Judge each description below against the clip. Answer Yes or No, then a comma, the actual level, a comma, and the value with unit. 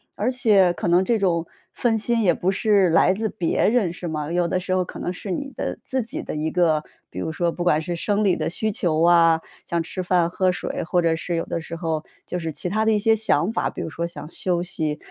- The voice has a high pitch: No, medium, 175 Hz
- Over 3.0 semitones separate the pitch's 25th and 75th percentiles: Yes, average, 3.4 semitones